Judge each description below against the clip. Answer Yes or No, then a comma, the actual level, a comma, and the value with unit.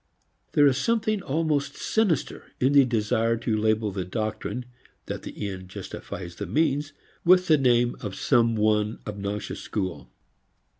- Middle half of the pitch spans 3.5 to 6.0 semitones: Yes, wide, 5.5 semitones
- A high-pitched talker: No, low, 115 Hz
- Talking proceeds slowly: No, average, 145 wpm